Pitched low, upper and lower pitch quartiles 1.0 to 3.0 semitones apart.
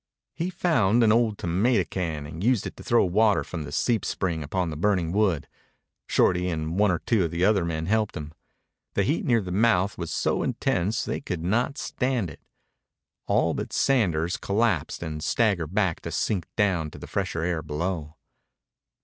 No: very low, 95 Hz; average, 4.8 semitones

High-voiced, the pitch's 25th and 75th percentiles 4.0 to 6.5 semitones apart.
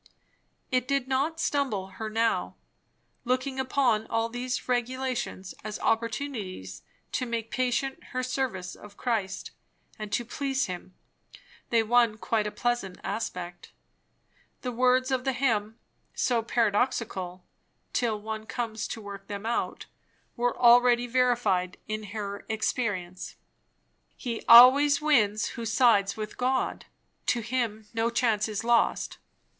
No: high, 230 Hz; average, 3.2 semitones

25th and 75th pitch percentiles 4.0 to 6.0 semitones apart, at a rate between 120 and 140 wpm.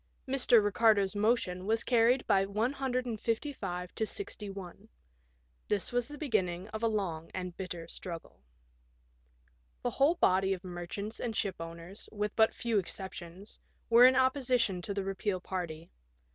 Yes: average, 4.4 semitones; slow, 135 wpm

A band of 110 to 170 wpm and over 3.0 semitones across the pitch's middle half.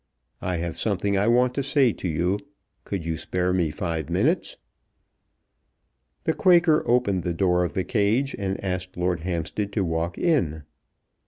Yes: average, 160 wpm; average, 5.1 semitones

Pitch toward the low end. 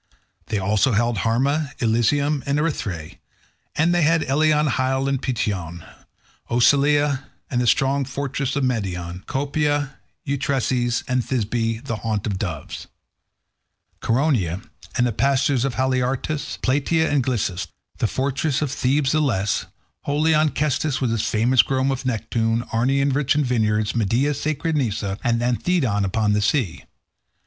Yes: low, 130 Hz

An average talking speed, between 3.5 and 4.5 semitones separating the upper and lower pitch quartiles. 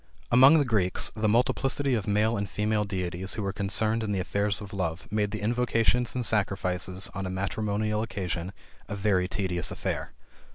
No: average, 175 wpm; average, 2.7 semitones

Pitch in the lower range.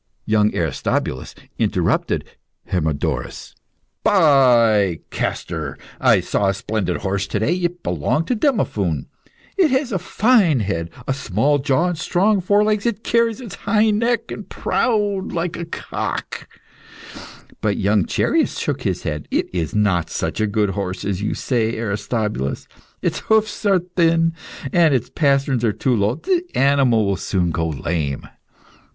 Yes: low, 125 Hz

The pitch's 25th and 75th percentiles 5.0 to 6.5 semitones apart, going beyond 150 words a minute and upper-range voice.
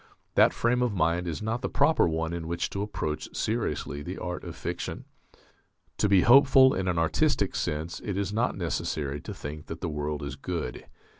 No: wide, 5.5 semitones; average, 195 wpm; very low, 85 Hz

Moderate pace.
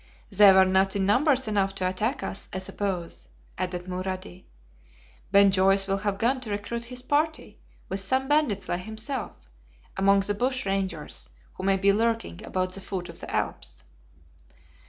Yes: average, 165 wpm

